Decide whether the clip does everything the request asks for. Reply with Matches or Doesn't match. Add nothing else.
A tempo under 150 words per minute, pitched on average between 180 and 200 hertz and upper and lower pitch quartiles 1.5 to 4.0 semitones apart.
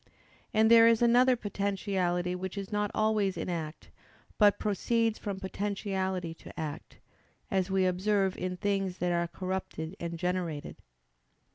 Matches